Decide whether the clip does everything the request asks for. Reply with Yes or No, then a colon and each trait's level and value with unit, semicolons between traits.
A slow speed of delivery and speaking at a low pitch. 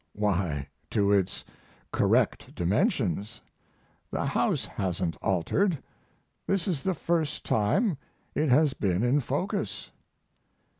Yes: slow, 105 wpm; low, 115 Hz